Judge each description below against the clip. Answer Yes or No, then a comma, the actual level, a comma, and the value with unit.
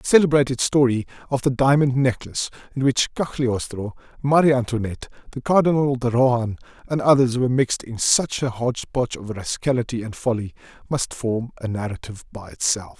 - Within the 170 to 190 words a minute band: No, average, 160 wpm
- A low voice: Yes, low, 125 Hz